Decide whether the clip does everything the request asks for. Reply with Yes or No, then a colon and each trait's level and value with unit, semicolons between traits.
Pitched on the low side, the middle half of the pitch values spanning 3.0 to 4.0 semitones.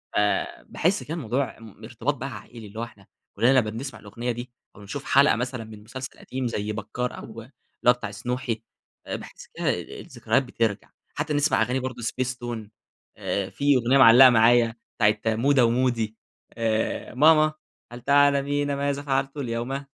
Yes: low, 120 Hz; average, 3.4 semitones